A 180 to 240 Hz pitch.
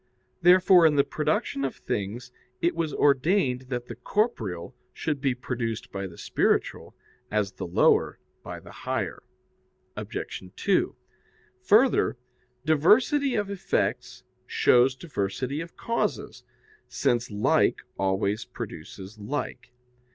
No: low, 130 Hz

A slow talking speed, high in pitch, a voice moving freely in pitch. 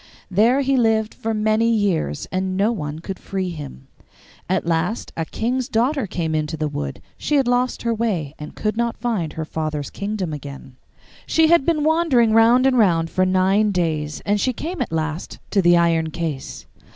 No: average, 190 wpm; high, 195 Hz; wide, 6.4 semitones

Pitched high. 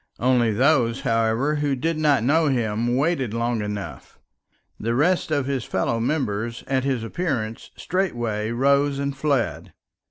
No: low, 130 Hz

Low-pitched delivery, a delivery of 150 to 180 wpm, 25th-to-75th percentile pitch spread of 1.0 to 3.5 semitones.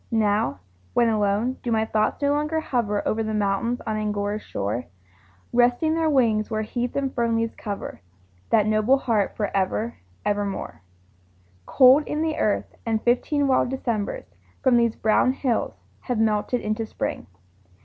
No: high, 225 Hz; average, 160 wpm; average, 3.2 semitones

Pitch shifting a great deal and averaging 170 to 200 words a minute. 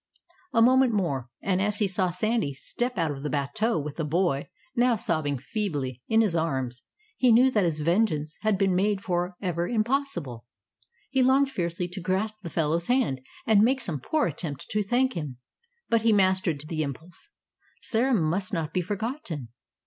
Yes: wide, 6.2 semitones; average, 180 wpm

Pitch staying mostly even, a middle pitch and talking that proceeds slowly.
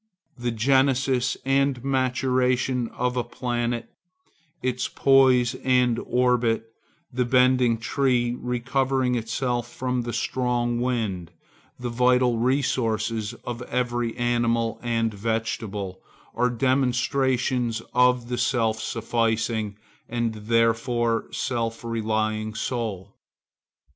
No: narrow, 1.7 semitones; low, 120 Hz; slow, 100 wpm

